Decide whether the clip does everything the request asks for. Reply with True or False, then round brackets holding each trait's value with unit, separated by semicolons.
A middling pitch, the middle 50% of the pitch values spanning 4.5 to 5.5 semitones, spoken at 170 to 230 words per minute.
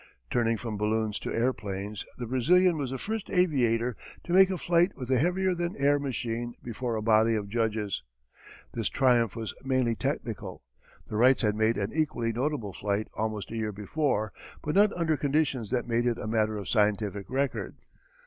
False (120 Hz; 4.8 semitones; 180 wpm)